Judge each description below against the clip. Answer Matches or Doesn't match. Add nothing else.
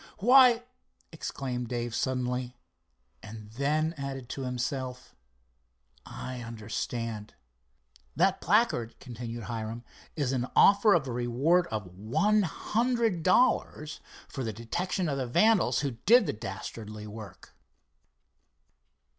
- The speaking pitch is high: Doesn't match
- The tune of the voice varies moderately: Doesn't match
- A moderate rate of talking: Doesn't match